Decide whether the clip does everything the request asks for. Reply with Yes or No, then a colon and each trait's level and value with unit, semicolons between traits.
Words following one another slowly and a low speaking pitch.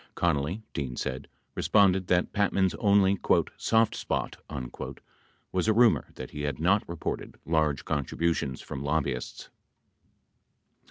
Yes: slow, 115 wpm; very low, 85 Hz